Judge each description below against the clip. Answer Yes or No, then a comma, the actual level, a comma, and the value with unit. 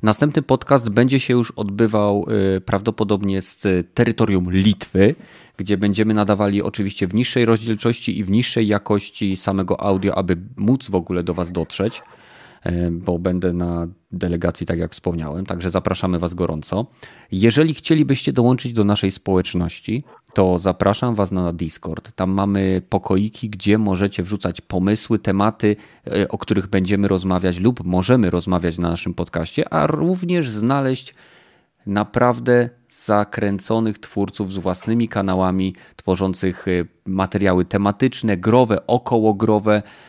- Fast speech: No, average, 125 wpm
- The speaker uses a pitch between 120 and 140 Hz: No, low, 100 Hz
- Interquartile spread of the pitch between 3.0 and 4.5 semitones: Yes, average, 3.4 semitones